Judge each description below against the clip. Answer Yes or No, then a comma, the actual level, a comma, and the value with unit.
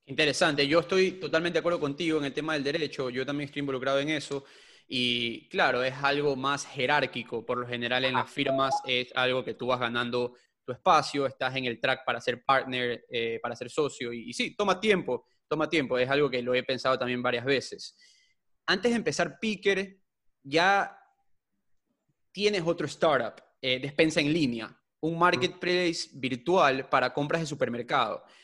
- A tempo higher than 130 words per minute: Yes, average, 175 wpm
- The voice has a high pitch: No, medium, 140 Hz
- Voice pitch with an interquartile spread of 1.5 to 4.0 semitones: No, average, 5.1 semitones